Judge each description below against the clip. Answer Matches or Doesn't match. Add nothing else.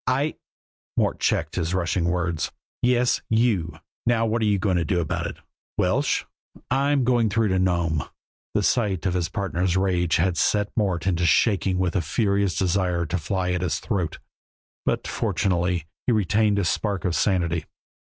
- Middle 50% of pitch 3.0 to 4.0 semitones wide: Matches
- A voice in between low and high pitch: Doesn't match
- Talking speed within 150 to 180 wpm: Matches